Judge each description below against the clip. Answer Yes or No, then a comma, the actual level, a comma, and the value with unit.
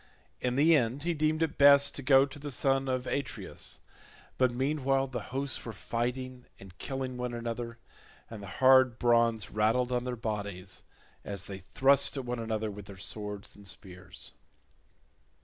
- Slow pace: No, average, 165 wpm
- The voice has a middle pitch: No, low, 125 Hz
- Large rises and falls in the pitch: No, average, 3.6 semitones